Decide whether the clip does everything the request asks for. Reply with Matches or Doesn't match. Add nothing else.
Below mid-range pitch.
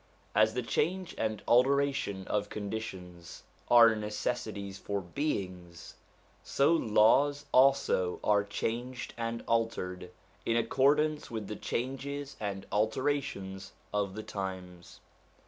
Matches